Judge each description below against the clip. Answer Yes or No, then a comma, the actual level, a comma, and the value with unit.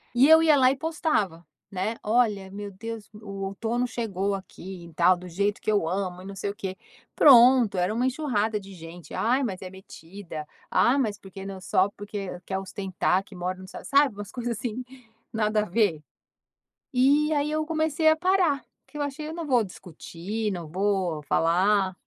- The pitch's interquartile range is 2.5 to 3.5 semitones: No, average, 5.0 semitones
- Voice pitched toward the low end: No, high, 205 Hz